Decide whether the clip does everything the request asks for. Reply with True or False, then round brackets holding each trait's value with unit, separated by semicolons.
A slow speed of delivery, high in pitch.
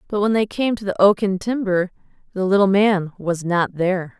False (200 wpm; 195 Hz)